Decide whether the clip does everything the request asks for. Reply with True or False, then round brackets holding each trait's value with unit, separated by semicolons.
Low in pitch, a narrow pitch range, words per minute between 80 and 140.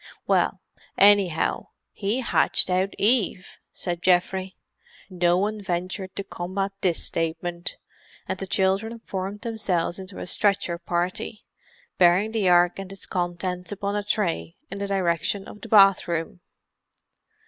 False (190 Hz; 2.3 semitones; 135 wpm)